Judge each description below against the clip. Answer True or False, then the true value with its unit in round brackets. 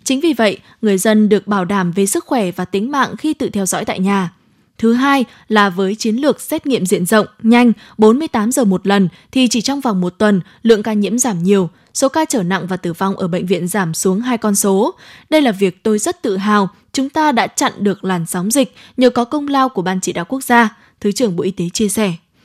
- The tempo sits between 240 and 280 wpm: True (250 wpm)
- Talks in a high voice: True (215 Hz)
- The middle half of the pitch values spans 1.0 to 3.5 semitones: False (4.3 semitones)